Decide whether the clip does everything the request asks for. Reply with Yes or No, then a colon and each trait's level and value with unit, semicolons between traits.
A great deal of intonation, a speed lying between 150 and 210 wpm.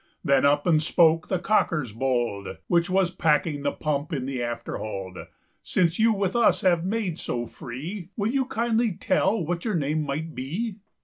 Yes: wide, 5.7 semitones; average, 160 wpm